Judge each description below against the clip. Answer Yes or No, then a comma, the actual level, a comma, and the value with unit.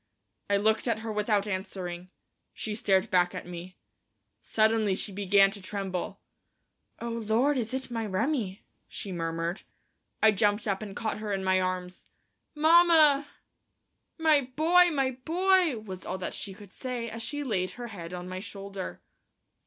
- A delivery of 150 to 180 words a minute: Yes, average, 160 wpm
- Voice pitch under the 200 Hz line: No, high, 210 Hz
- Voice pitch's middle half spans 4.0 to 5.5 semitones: Yes, average, 4.7 semitones